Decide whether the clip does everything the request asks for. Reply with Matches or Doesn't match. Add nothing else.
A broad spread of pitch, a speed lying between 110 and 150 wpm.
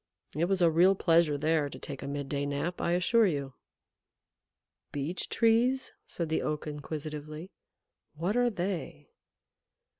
Doesn't match